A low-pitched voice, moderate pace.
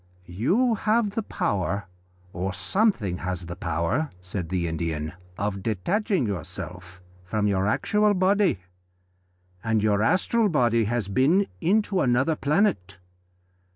No: low, 110 Hz; slow, 120 wpm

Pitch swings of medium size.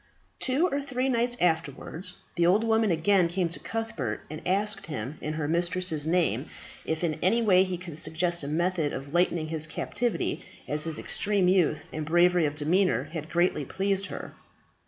Yes: average, 3.8 semitones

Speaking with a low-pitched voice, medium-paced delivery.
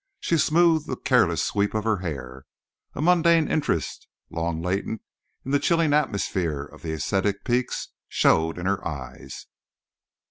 Yes: low, 100 Hz; average, 145 wpm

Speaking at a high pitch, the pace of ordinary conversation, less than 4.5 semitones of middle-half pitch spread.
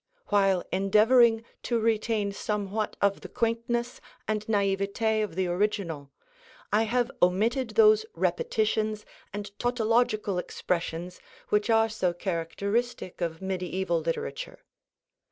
No: high, 210 Hz; slow, 110 wpm; average, 3.3 semitones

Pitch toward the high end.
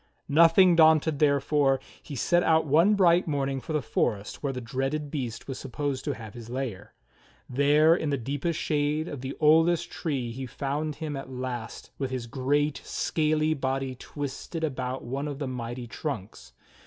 No: medium, 140 Hz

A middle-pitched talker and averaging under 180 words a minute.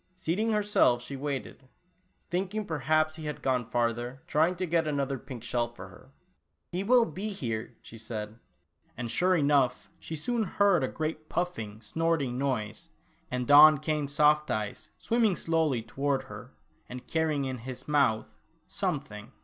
Yes: medium, 145 Hz; average, 160 wpm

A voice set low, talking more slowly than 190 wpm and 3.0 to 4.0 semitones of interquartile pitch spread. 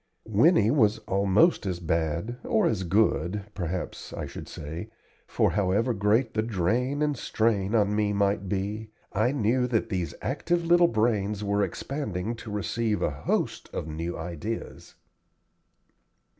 Yes: low, 105 Hz; average, 145 wpm; average, 3.6 semitones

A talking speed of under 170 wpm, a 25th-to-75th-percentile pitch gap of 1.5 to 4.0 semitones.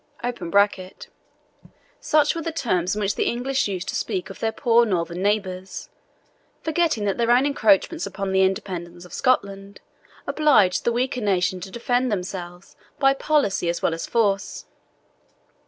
No: average, 150 wpm; average, 5.2 semitones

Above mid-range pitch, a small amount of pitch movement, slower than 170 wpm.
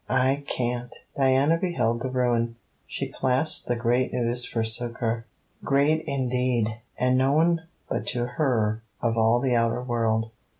No: low, 125 Hz; narrow, 2.2 semitones; average, 140 wpm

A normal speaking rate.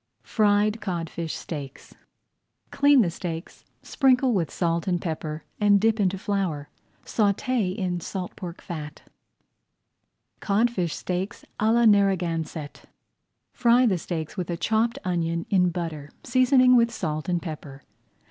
No: slow, 130 wpm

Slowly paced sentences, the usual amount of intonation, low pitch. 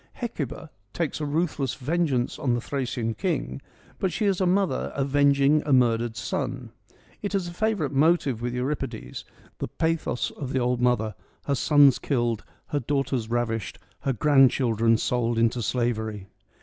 No: average, 150 wpm; average, 3.8 semitones; low, 130 Hz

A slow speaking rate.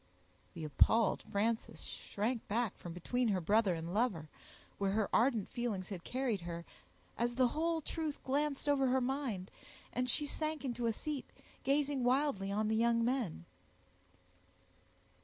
No: average, 150 wpm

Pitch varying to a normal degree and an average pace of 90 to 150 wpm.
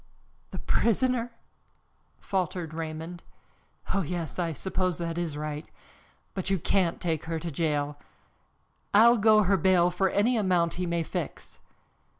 Yes: average, 3.0 semitones; average, 140 wpm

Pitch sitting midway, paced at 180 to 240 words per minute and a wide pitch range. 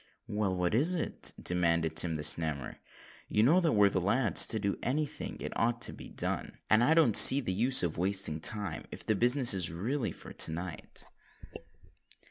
No: low, 100 Hz; average, 195 wpm; wide, 6.0 semitones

